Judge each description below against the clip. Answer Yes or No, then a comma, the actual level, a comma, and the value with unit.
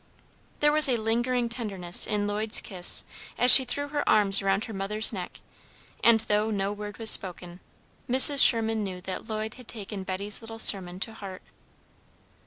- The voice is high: Yes, high, 215 Hz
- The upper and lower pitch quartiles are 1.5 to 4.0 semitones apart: Yes, average, 3.0 semitones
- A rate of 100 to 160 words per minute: No, average, 170 wpm